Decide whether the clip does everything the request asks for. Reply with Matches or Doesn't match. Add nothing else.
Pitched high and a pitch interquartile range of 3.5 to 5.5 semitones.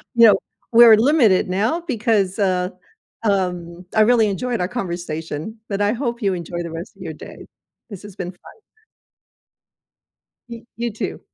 Matches